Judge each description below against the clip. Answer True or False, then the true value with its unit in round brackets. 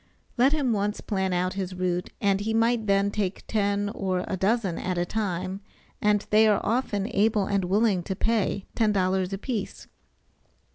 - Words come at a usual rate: True (175 wpm)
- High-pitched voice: True (200 Hz)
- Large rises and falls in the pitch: False (2.5 semitones)